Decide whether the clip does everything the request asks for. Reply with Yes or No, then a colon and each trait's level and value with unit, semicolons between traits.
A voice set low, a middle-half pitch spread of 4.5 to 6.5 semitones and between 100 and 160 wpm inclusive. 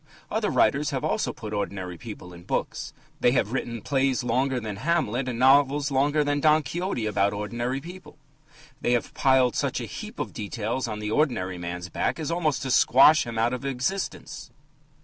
No: low, 125 Hz; average, 5.0 semitones; average, 185 wpm